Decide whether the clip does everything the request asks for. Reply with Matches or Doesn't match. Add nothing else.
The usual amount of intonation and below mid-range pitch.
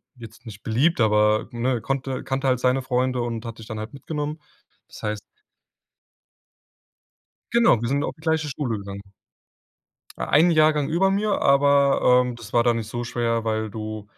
Matches